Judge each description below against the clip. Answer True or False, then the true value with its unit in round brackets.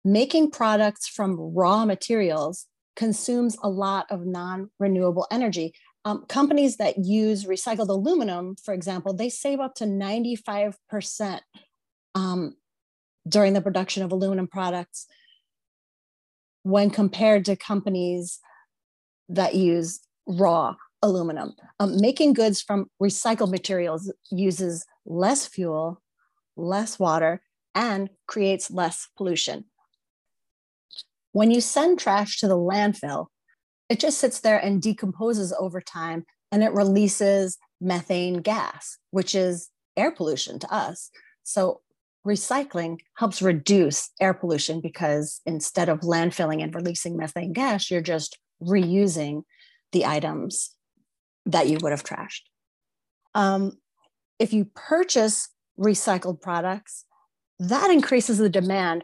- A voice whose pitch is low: False (195 Hz)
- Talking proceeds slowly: True (115 wpm)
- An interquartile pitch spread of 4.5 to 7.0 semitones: False (3.3 semitones)